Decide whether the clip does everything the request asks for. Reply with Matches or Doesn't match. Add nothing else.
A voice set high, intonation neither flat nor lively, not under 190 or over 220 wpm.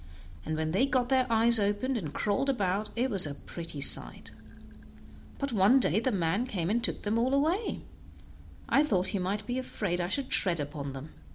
Doesn't match